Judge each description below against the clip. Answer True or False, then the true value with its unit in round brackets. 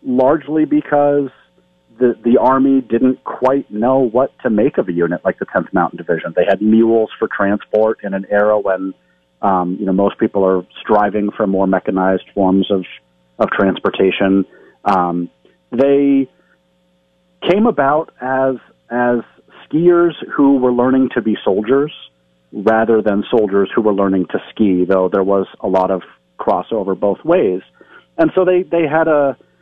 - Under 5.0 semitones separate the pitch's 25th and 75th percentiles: False (5.6 semitones)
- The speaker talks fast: False (160 wpm)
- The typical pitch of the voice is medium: False (105 Hz)